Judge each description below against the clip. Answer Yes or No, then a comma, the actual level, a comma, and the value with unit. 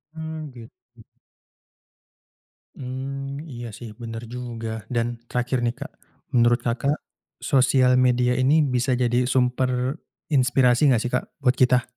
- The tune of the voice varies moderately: No, narrow, 1.7 semitones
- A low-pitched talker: Yes, low, 125 Hz